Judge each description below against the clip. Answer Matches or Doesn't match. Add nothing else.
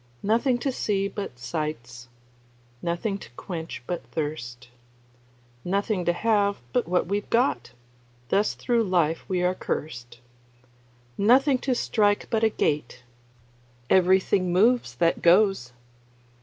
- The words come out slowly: Matches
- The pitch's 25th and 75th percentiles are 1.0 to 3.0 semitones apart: Doesn't match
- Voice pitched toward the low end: Doesn't match